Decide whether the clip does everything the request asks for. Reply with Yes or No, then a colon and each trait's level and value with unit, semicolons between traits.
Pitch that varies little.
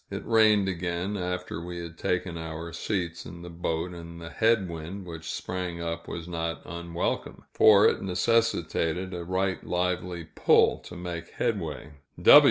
Yes: narrow, 1.8 semitones